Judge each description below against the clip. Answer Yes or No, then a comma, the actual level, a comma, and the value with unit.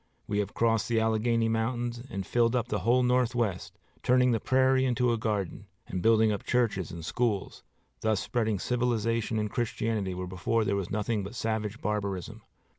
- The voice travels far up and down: No, average, 2.7 semitones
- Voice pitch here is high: No, low, 115 Hz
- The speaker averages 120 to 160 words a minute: No, average, 175 wpm